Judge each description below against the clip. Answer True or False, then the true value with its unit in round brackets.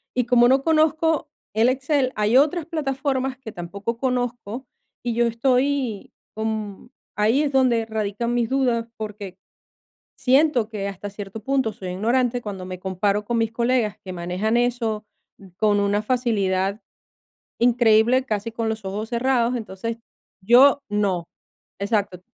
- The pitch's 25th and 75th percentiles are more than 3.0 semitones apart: True (3.7 semitones)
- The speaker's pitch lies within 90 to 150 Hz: False (230 Hz)